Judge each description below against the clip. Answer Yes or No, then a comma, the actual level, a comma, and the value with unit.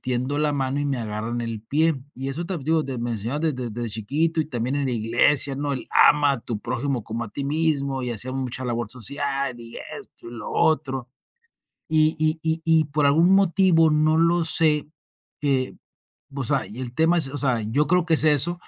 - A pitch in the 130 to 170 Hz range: Yes, medium, 140 Hz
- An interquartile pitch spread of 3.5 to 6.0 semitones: Yes, average, 4.3 semitones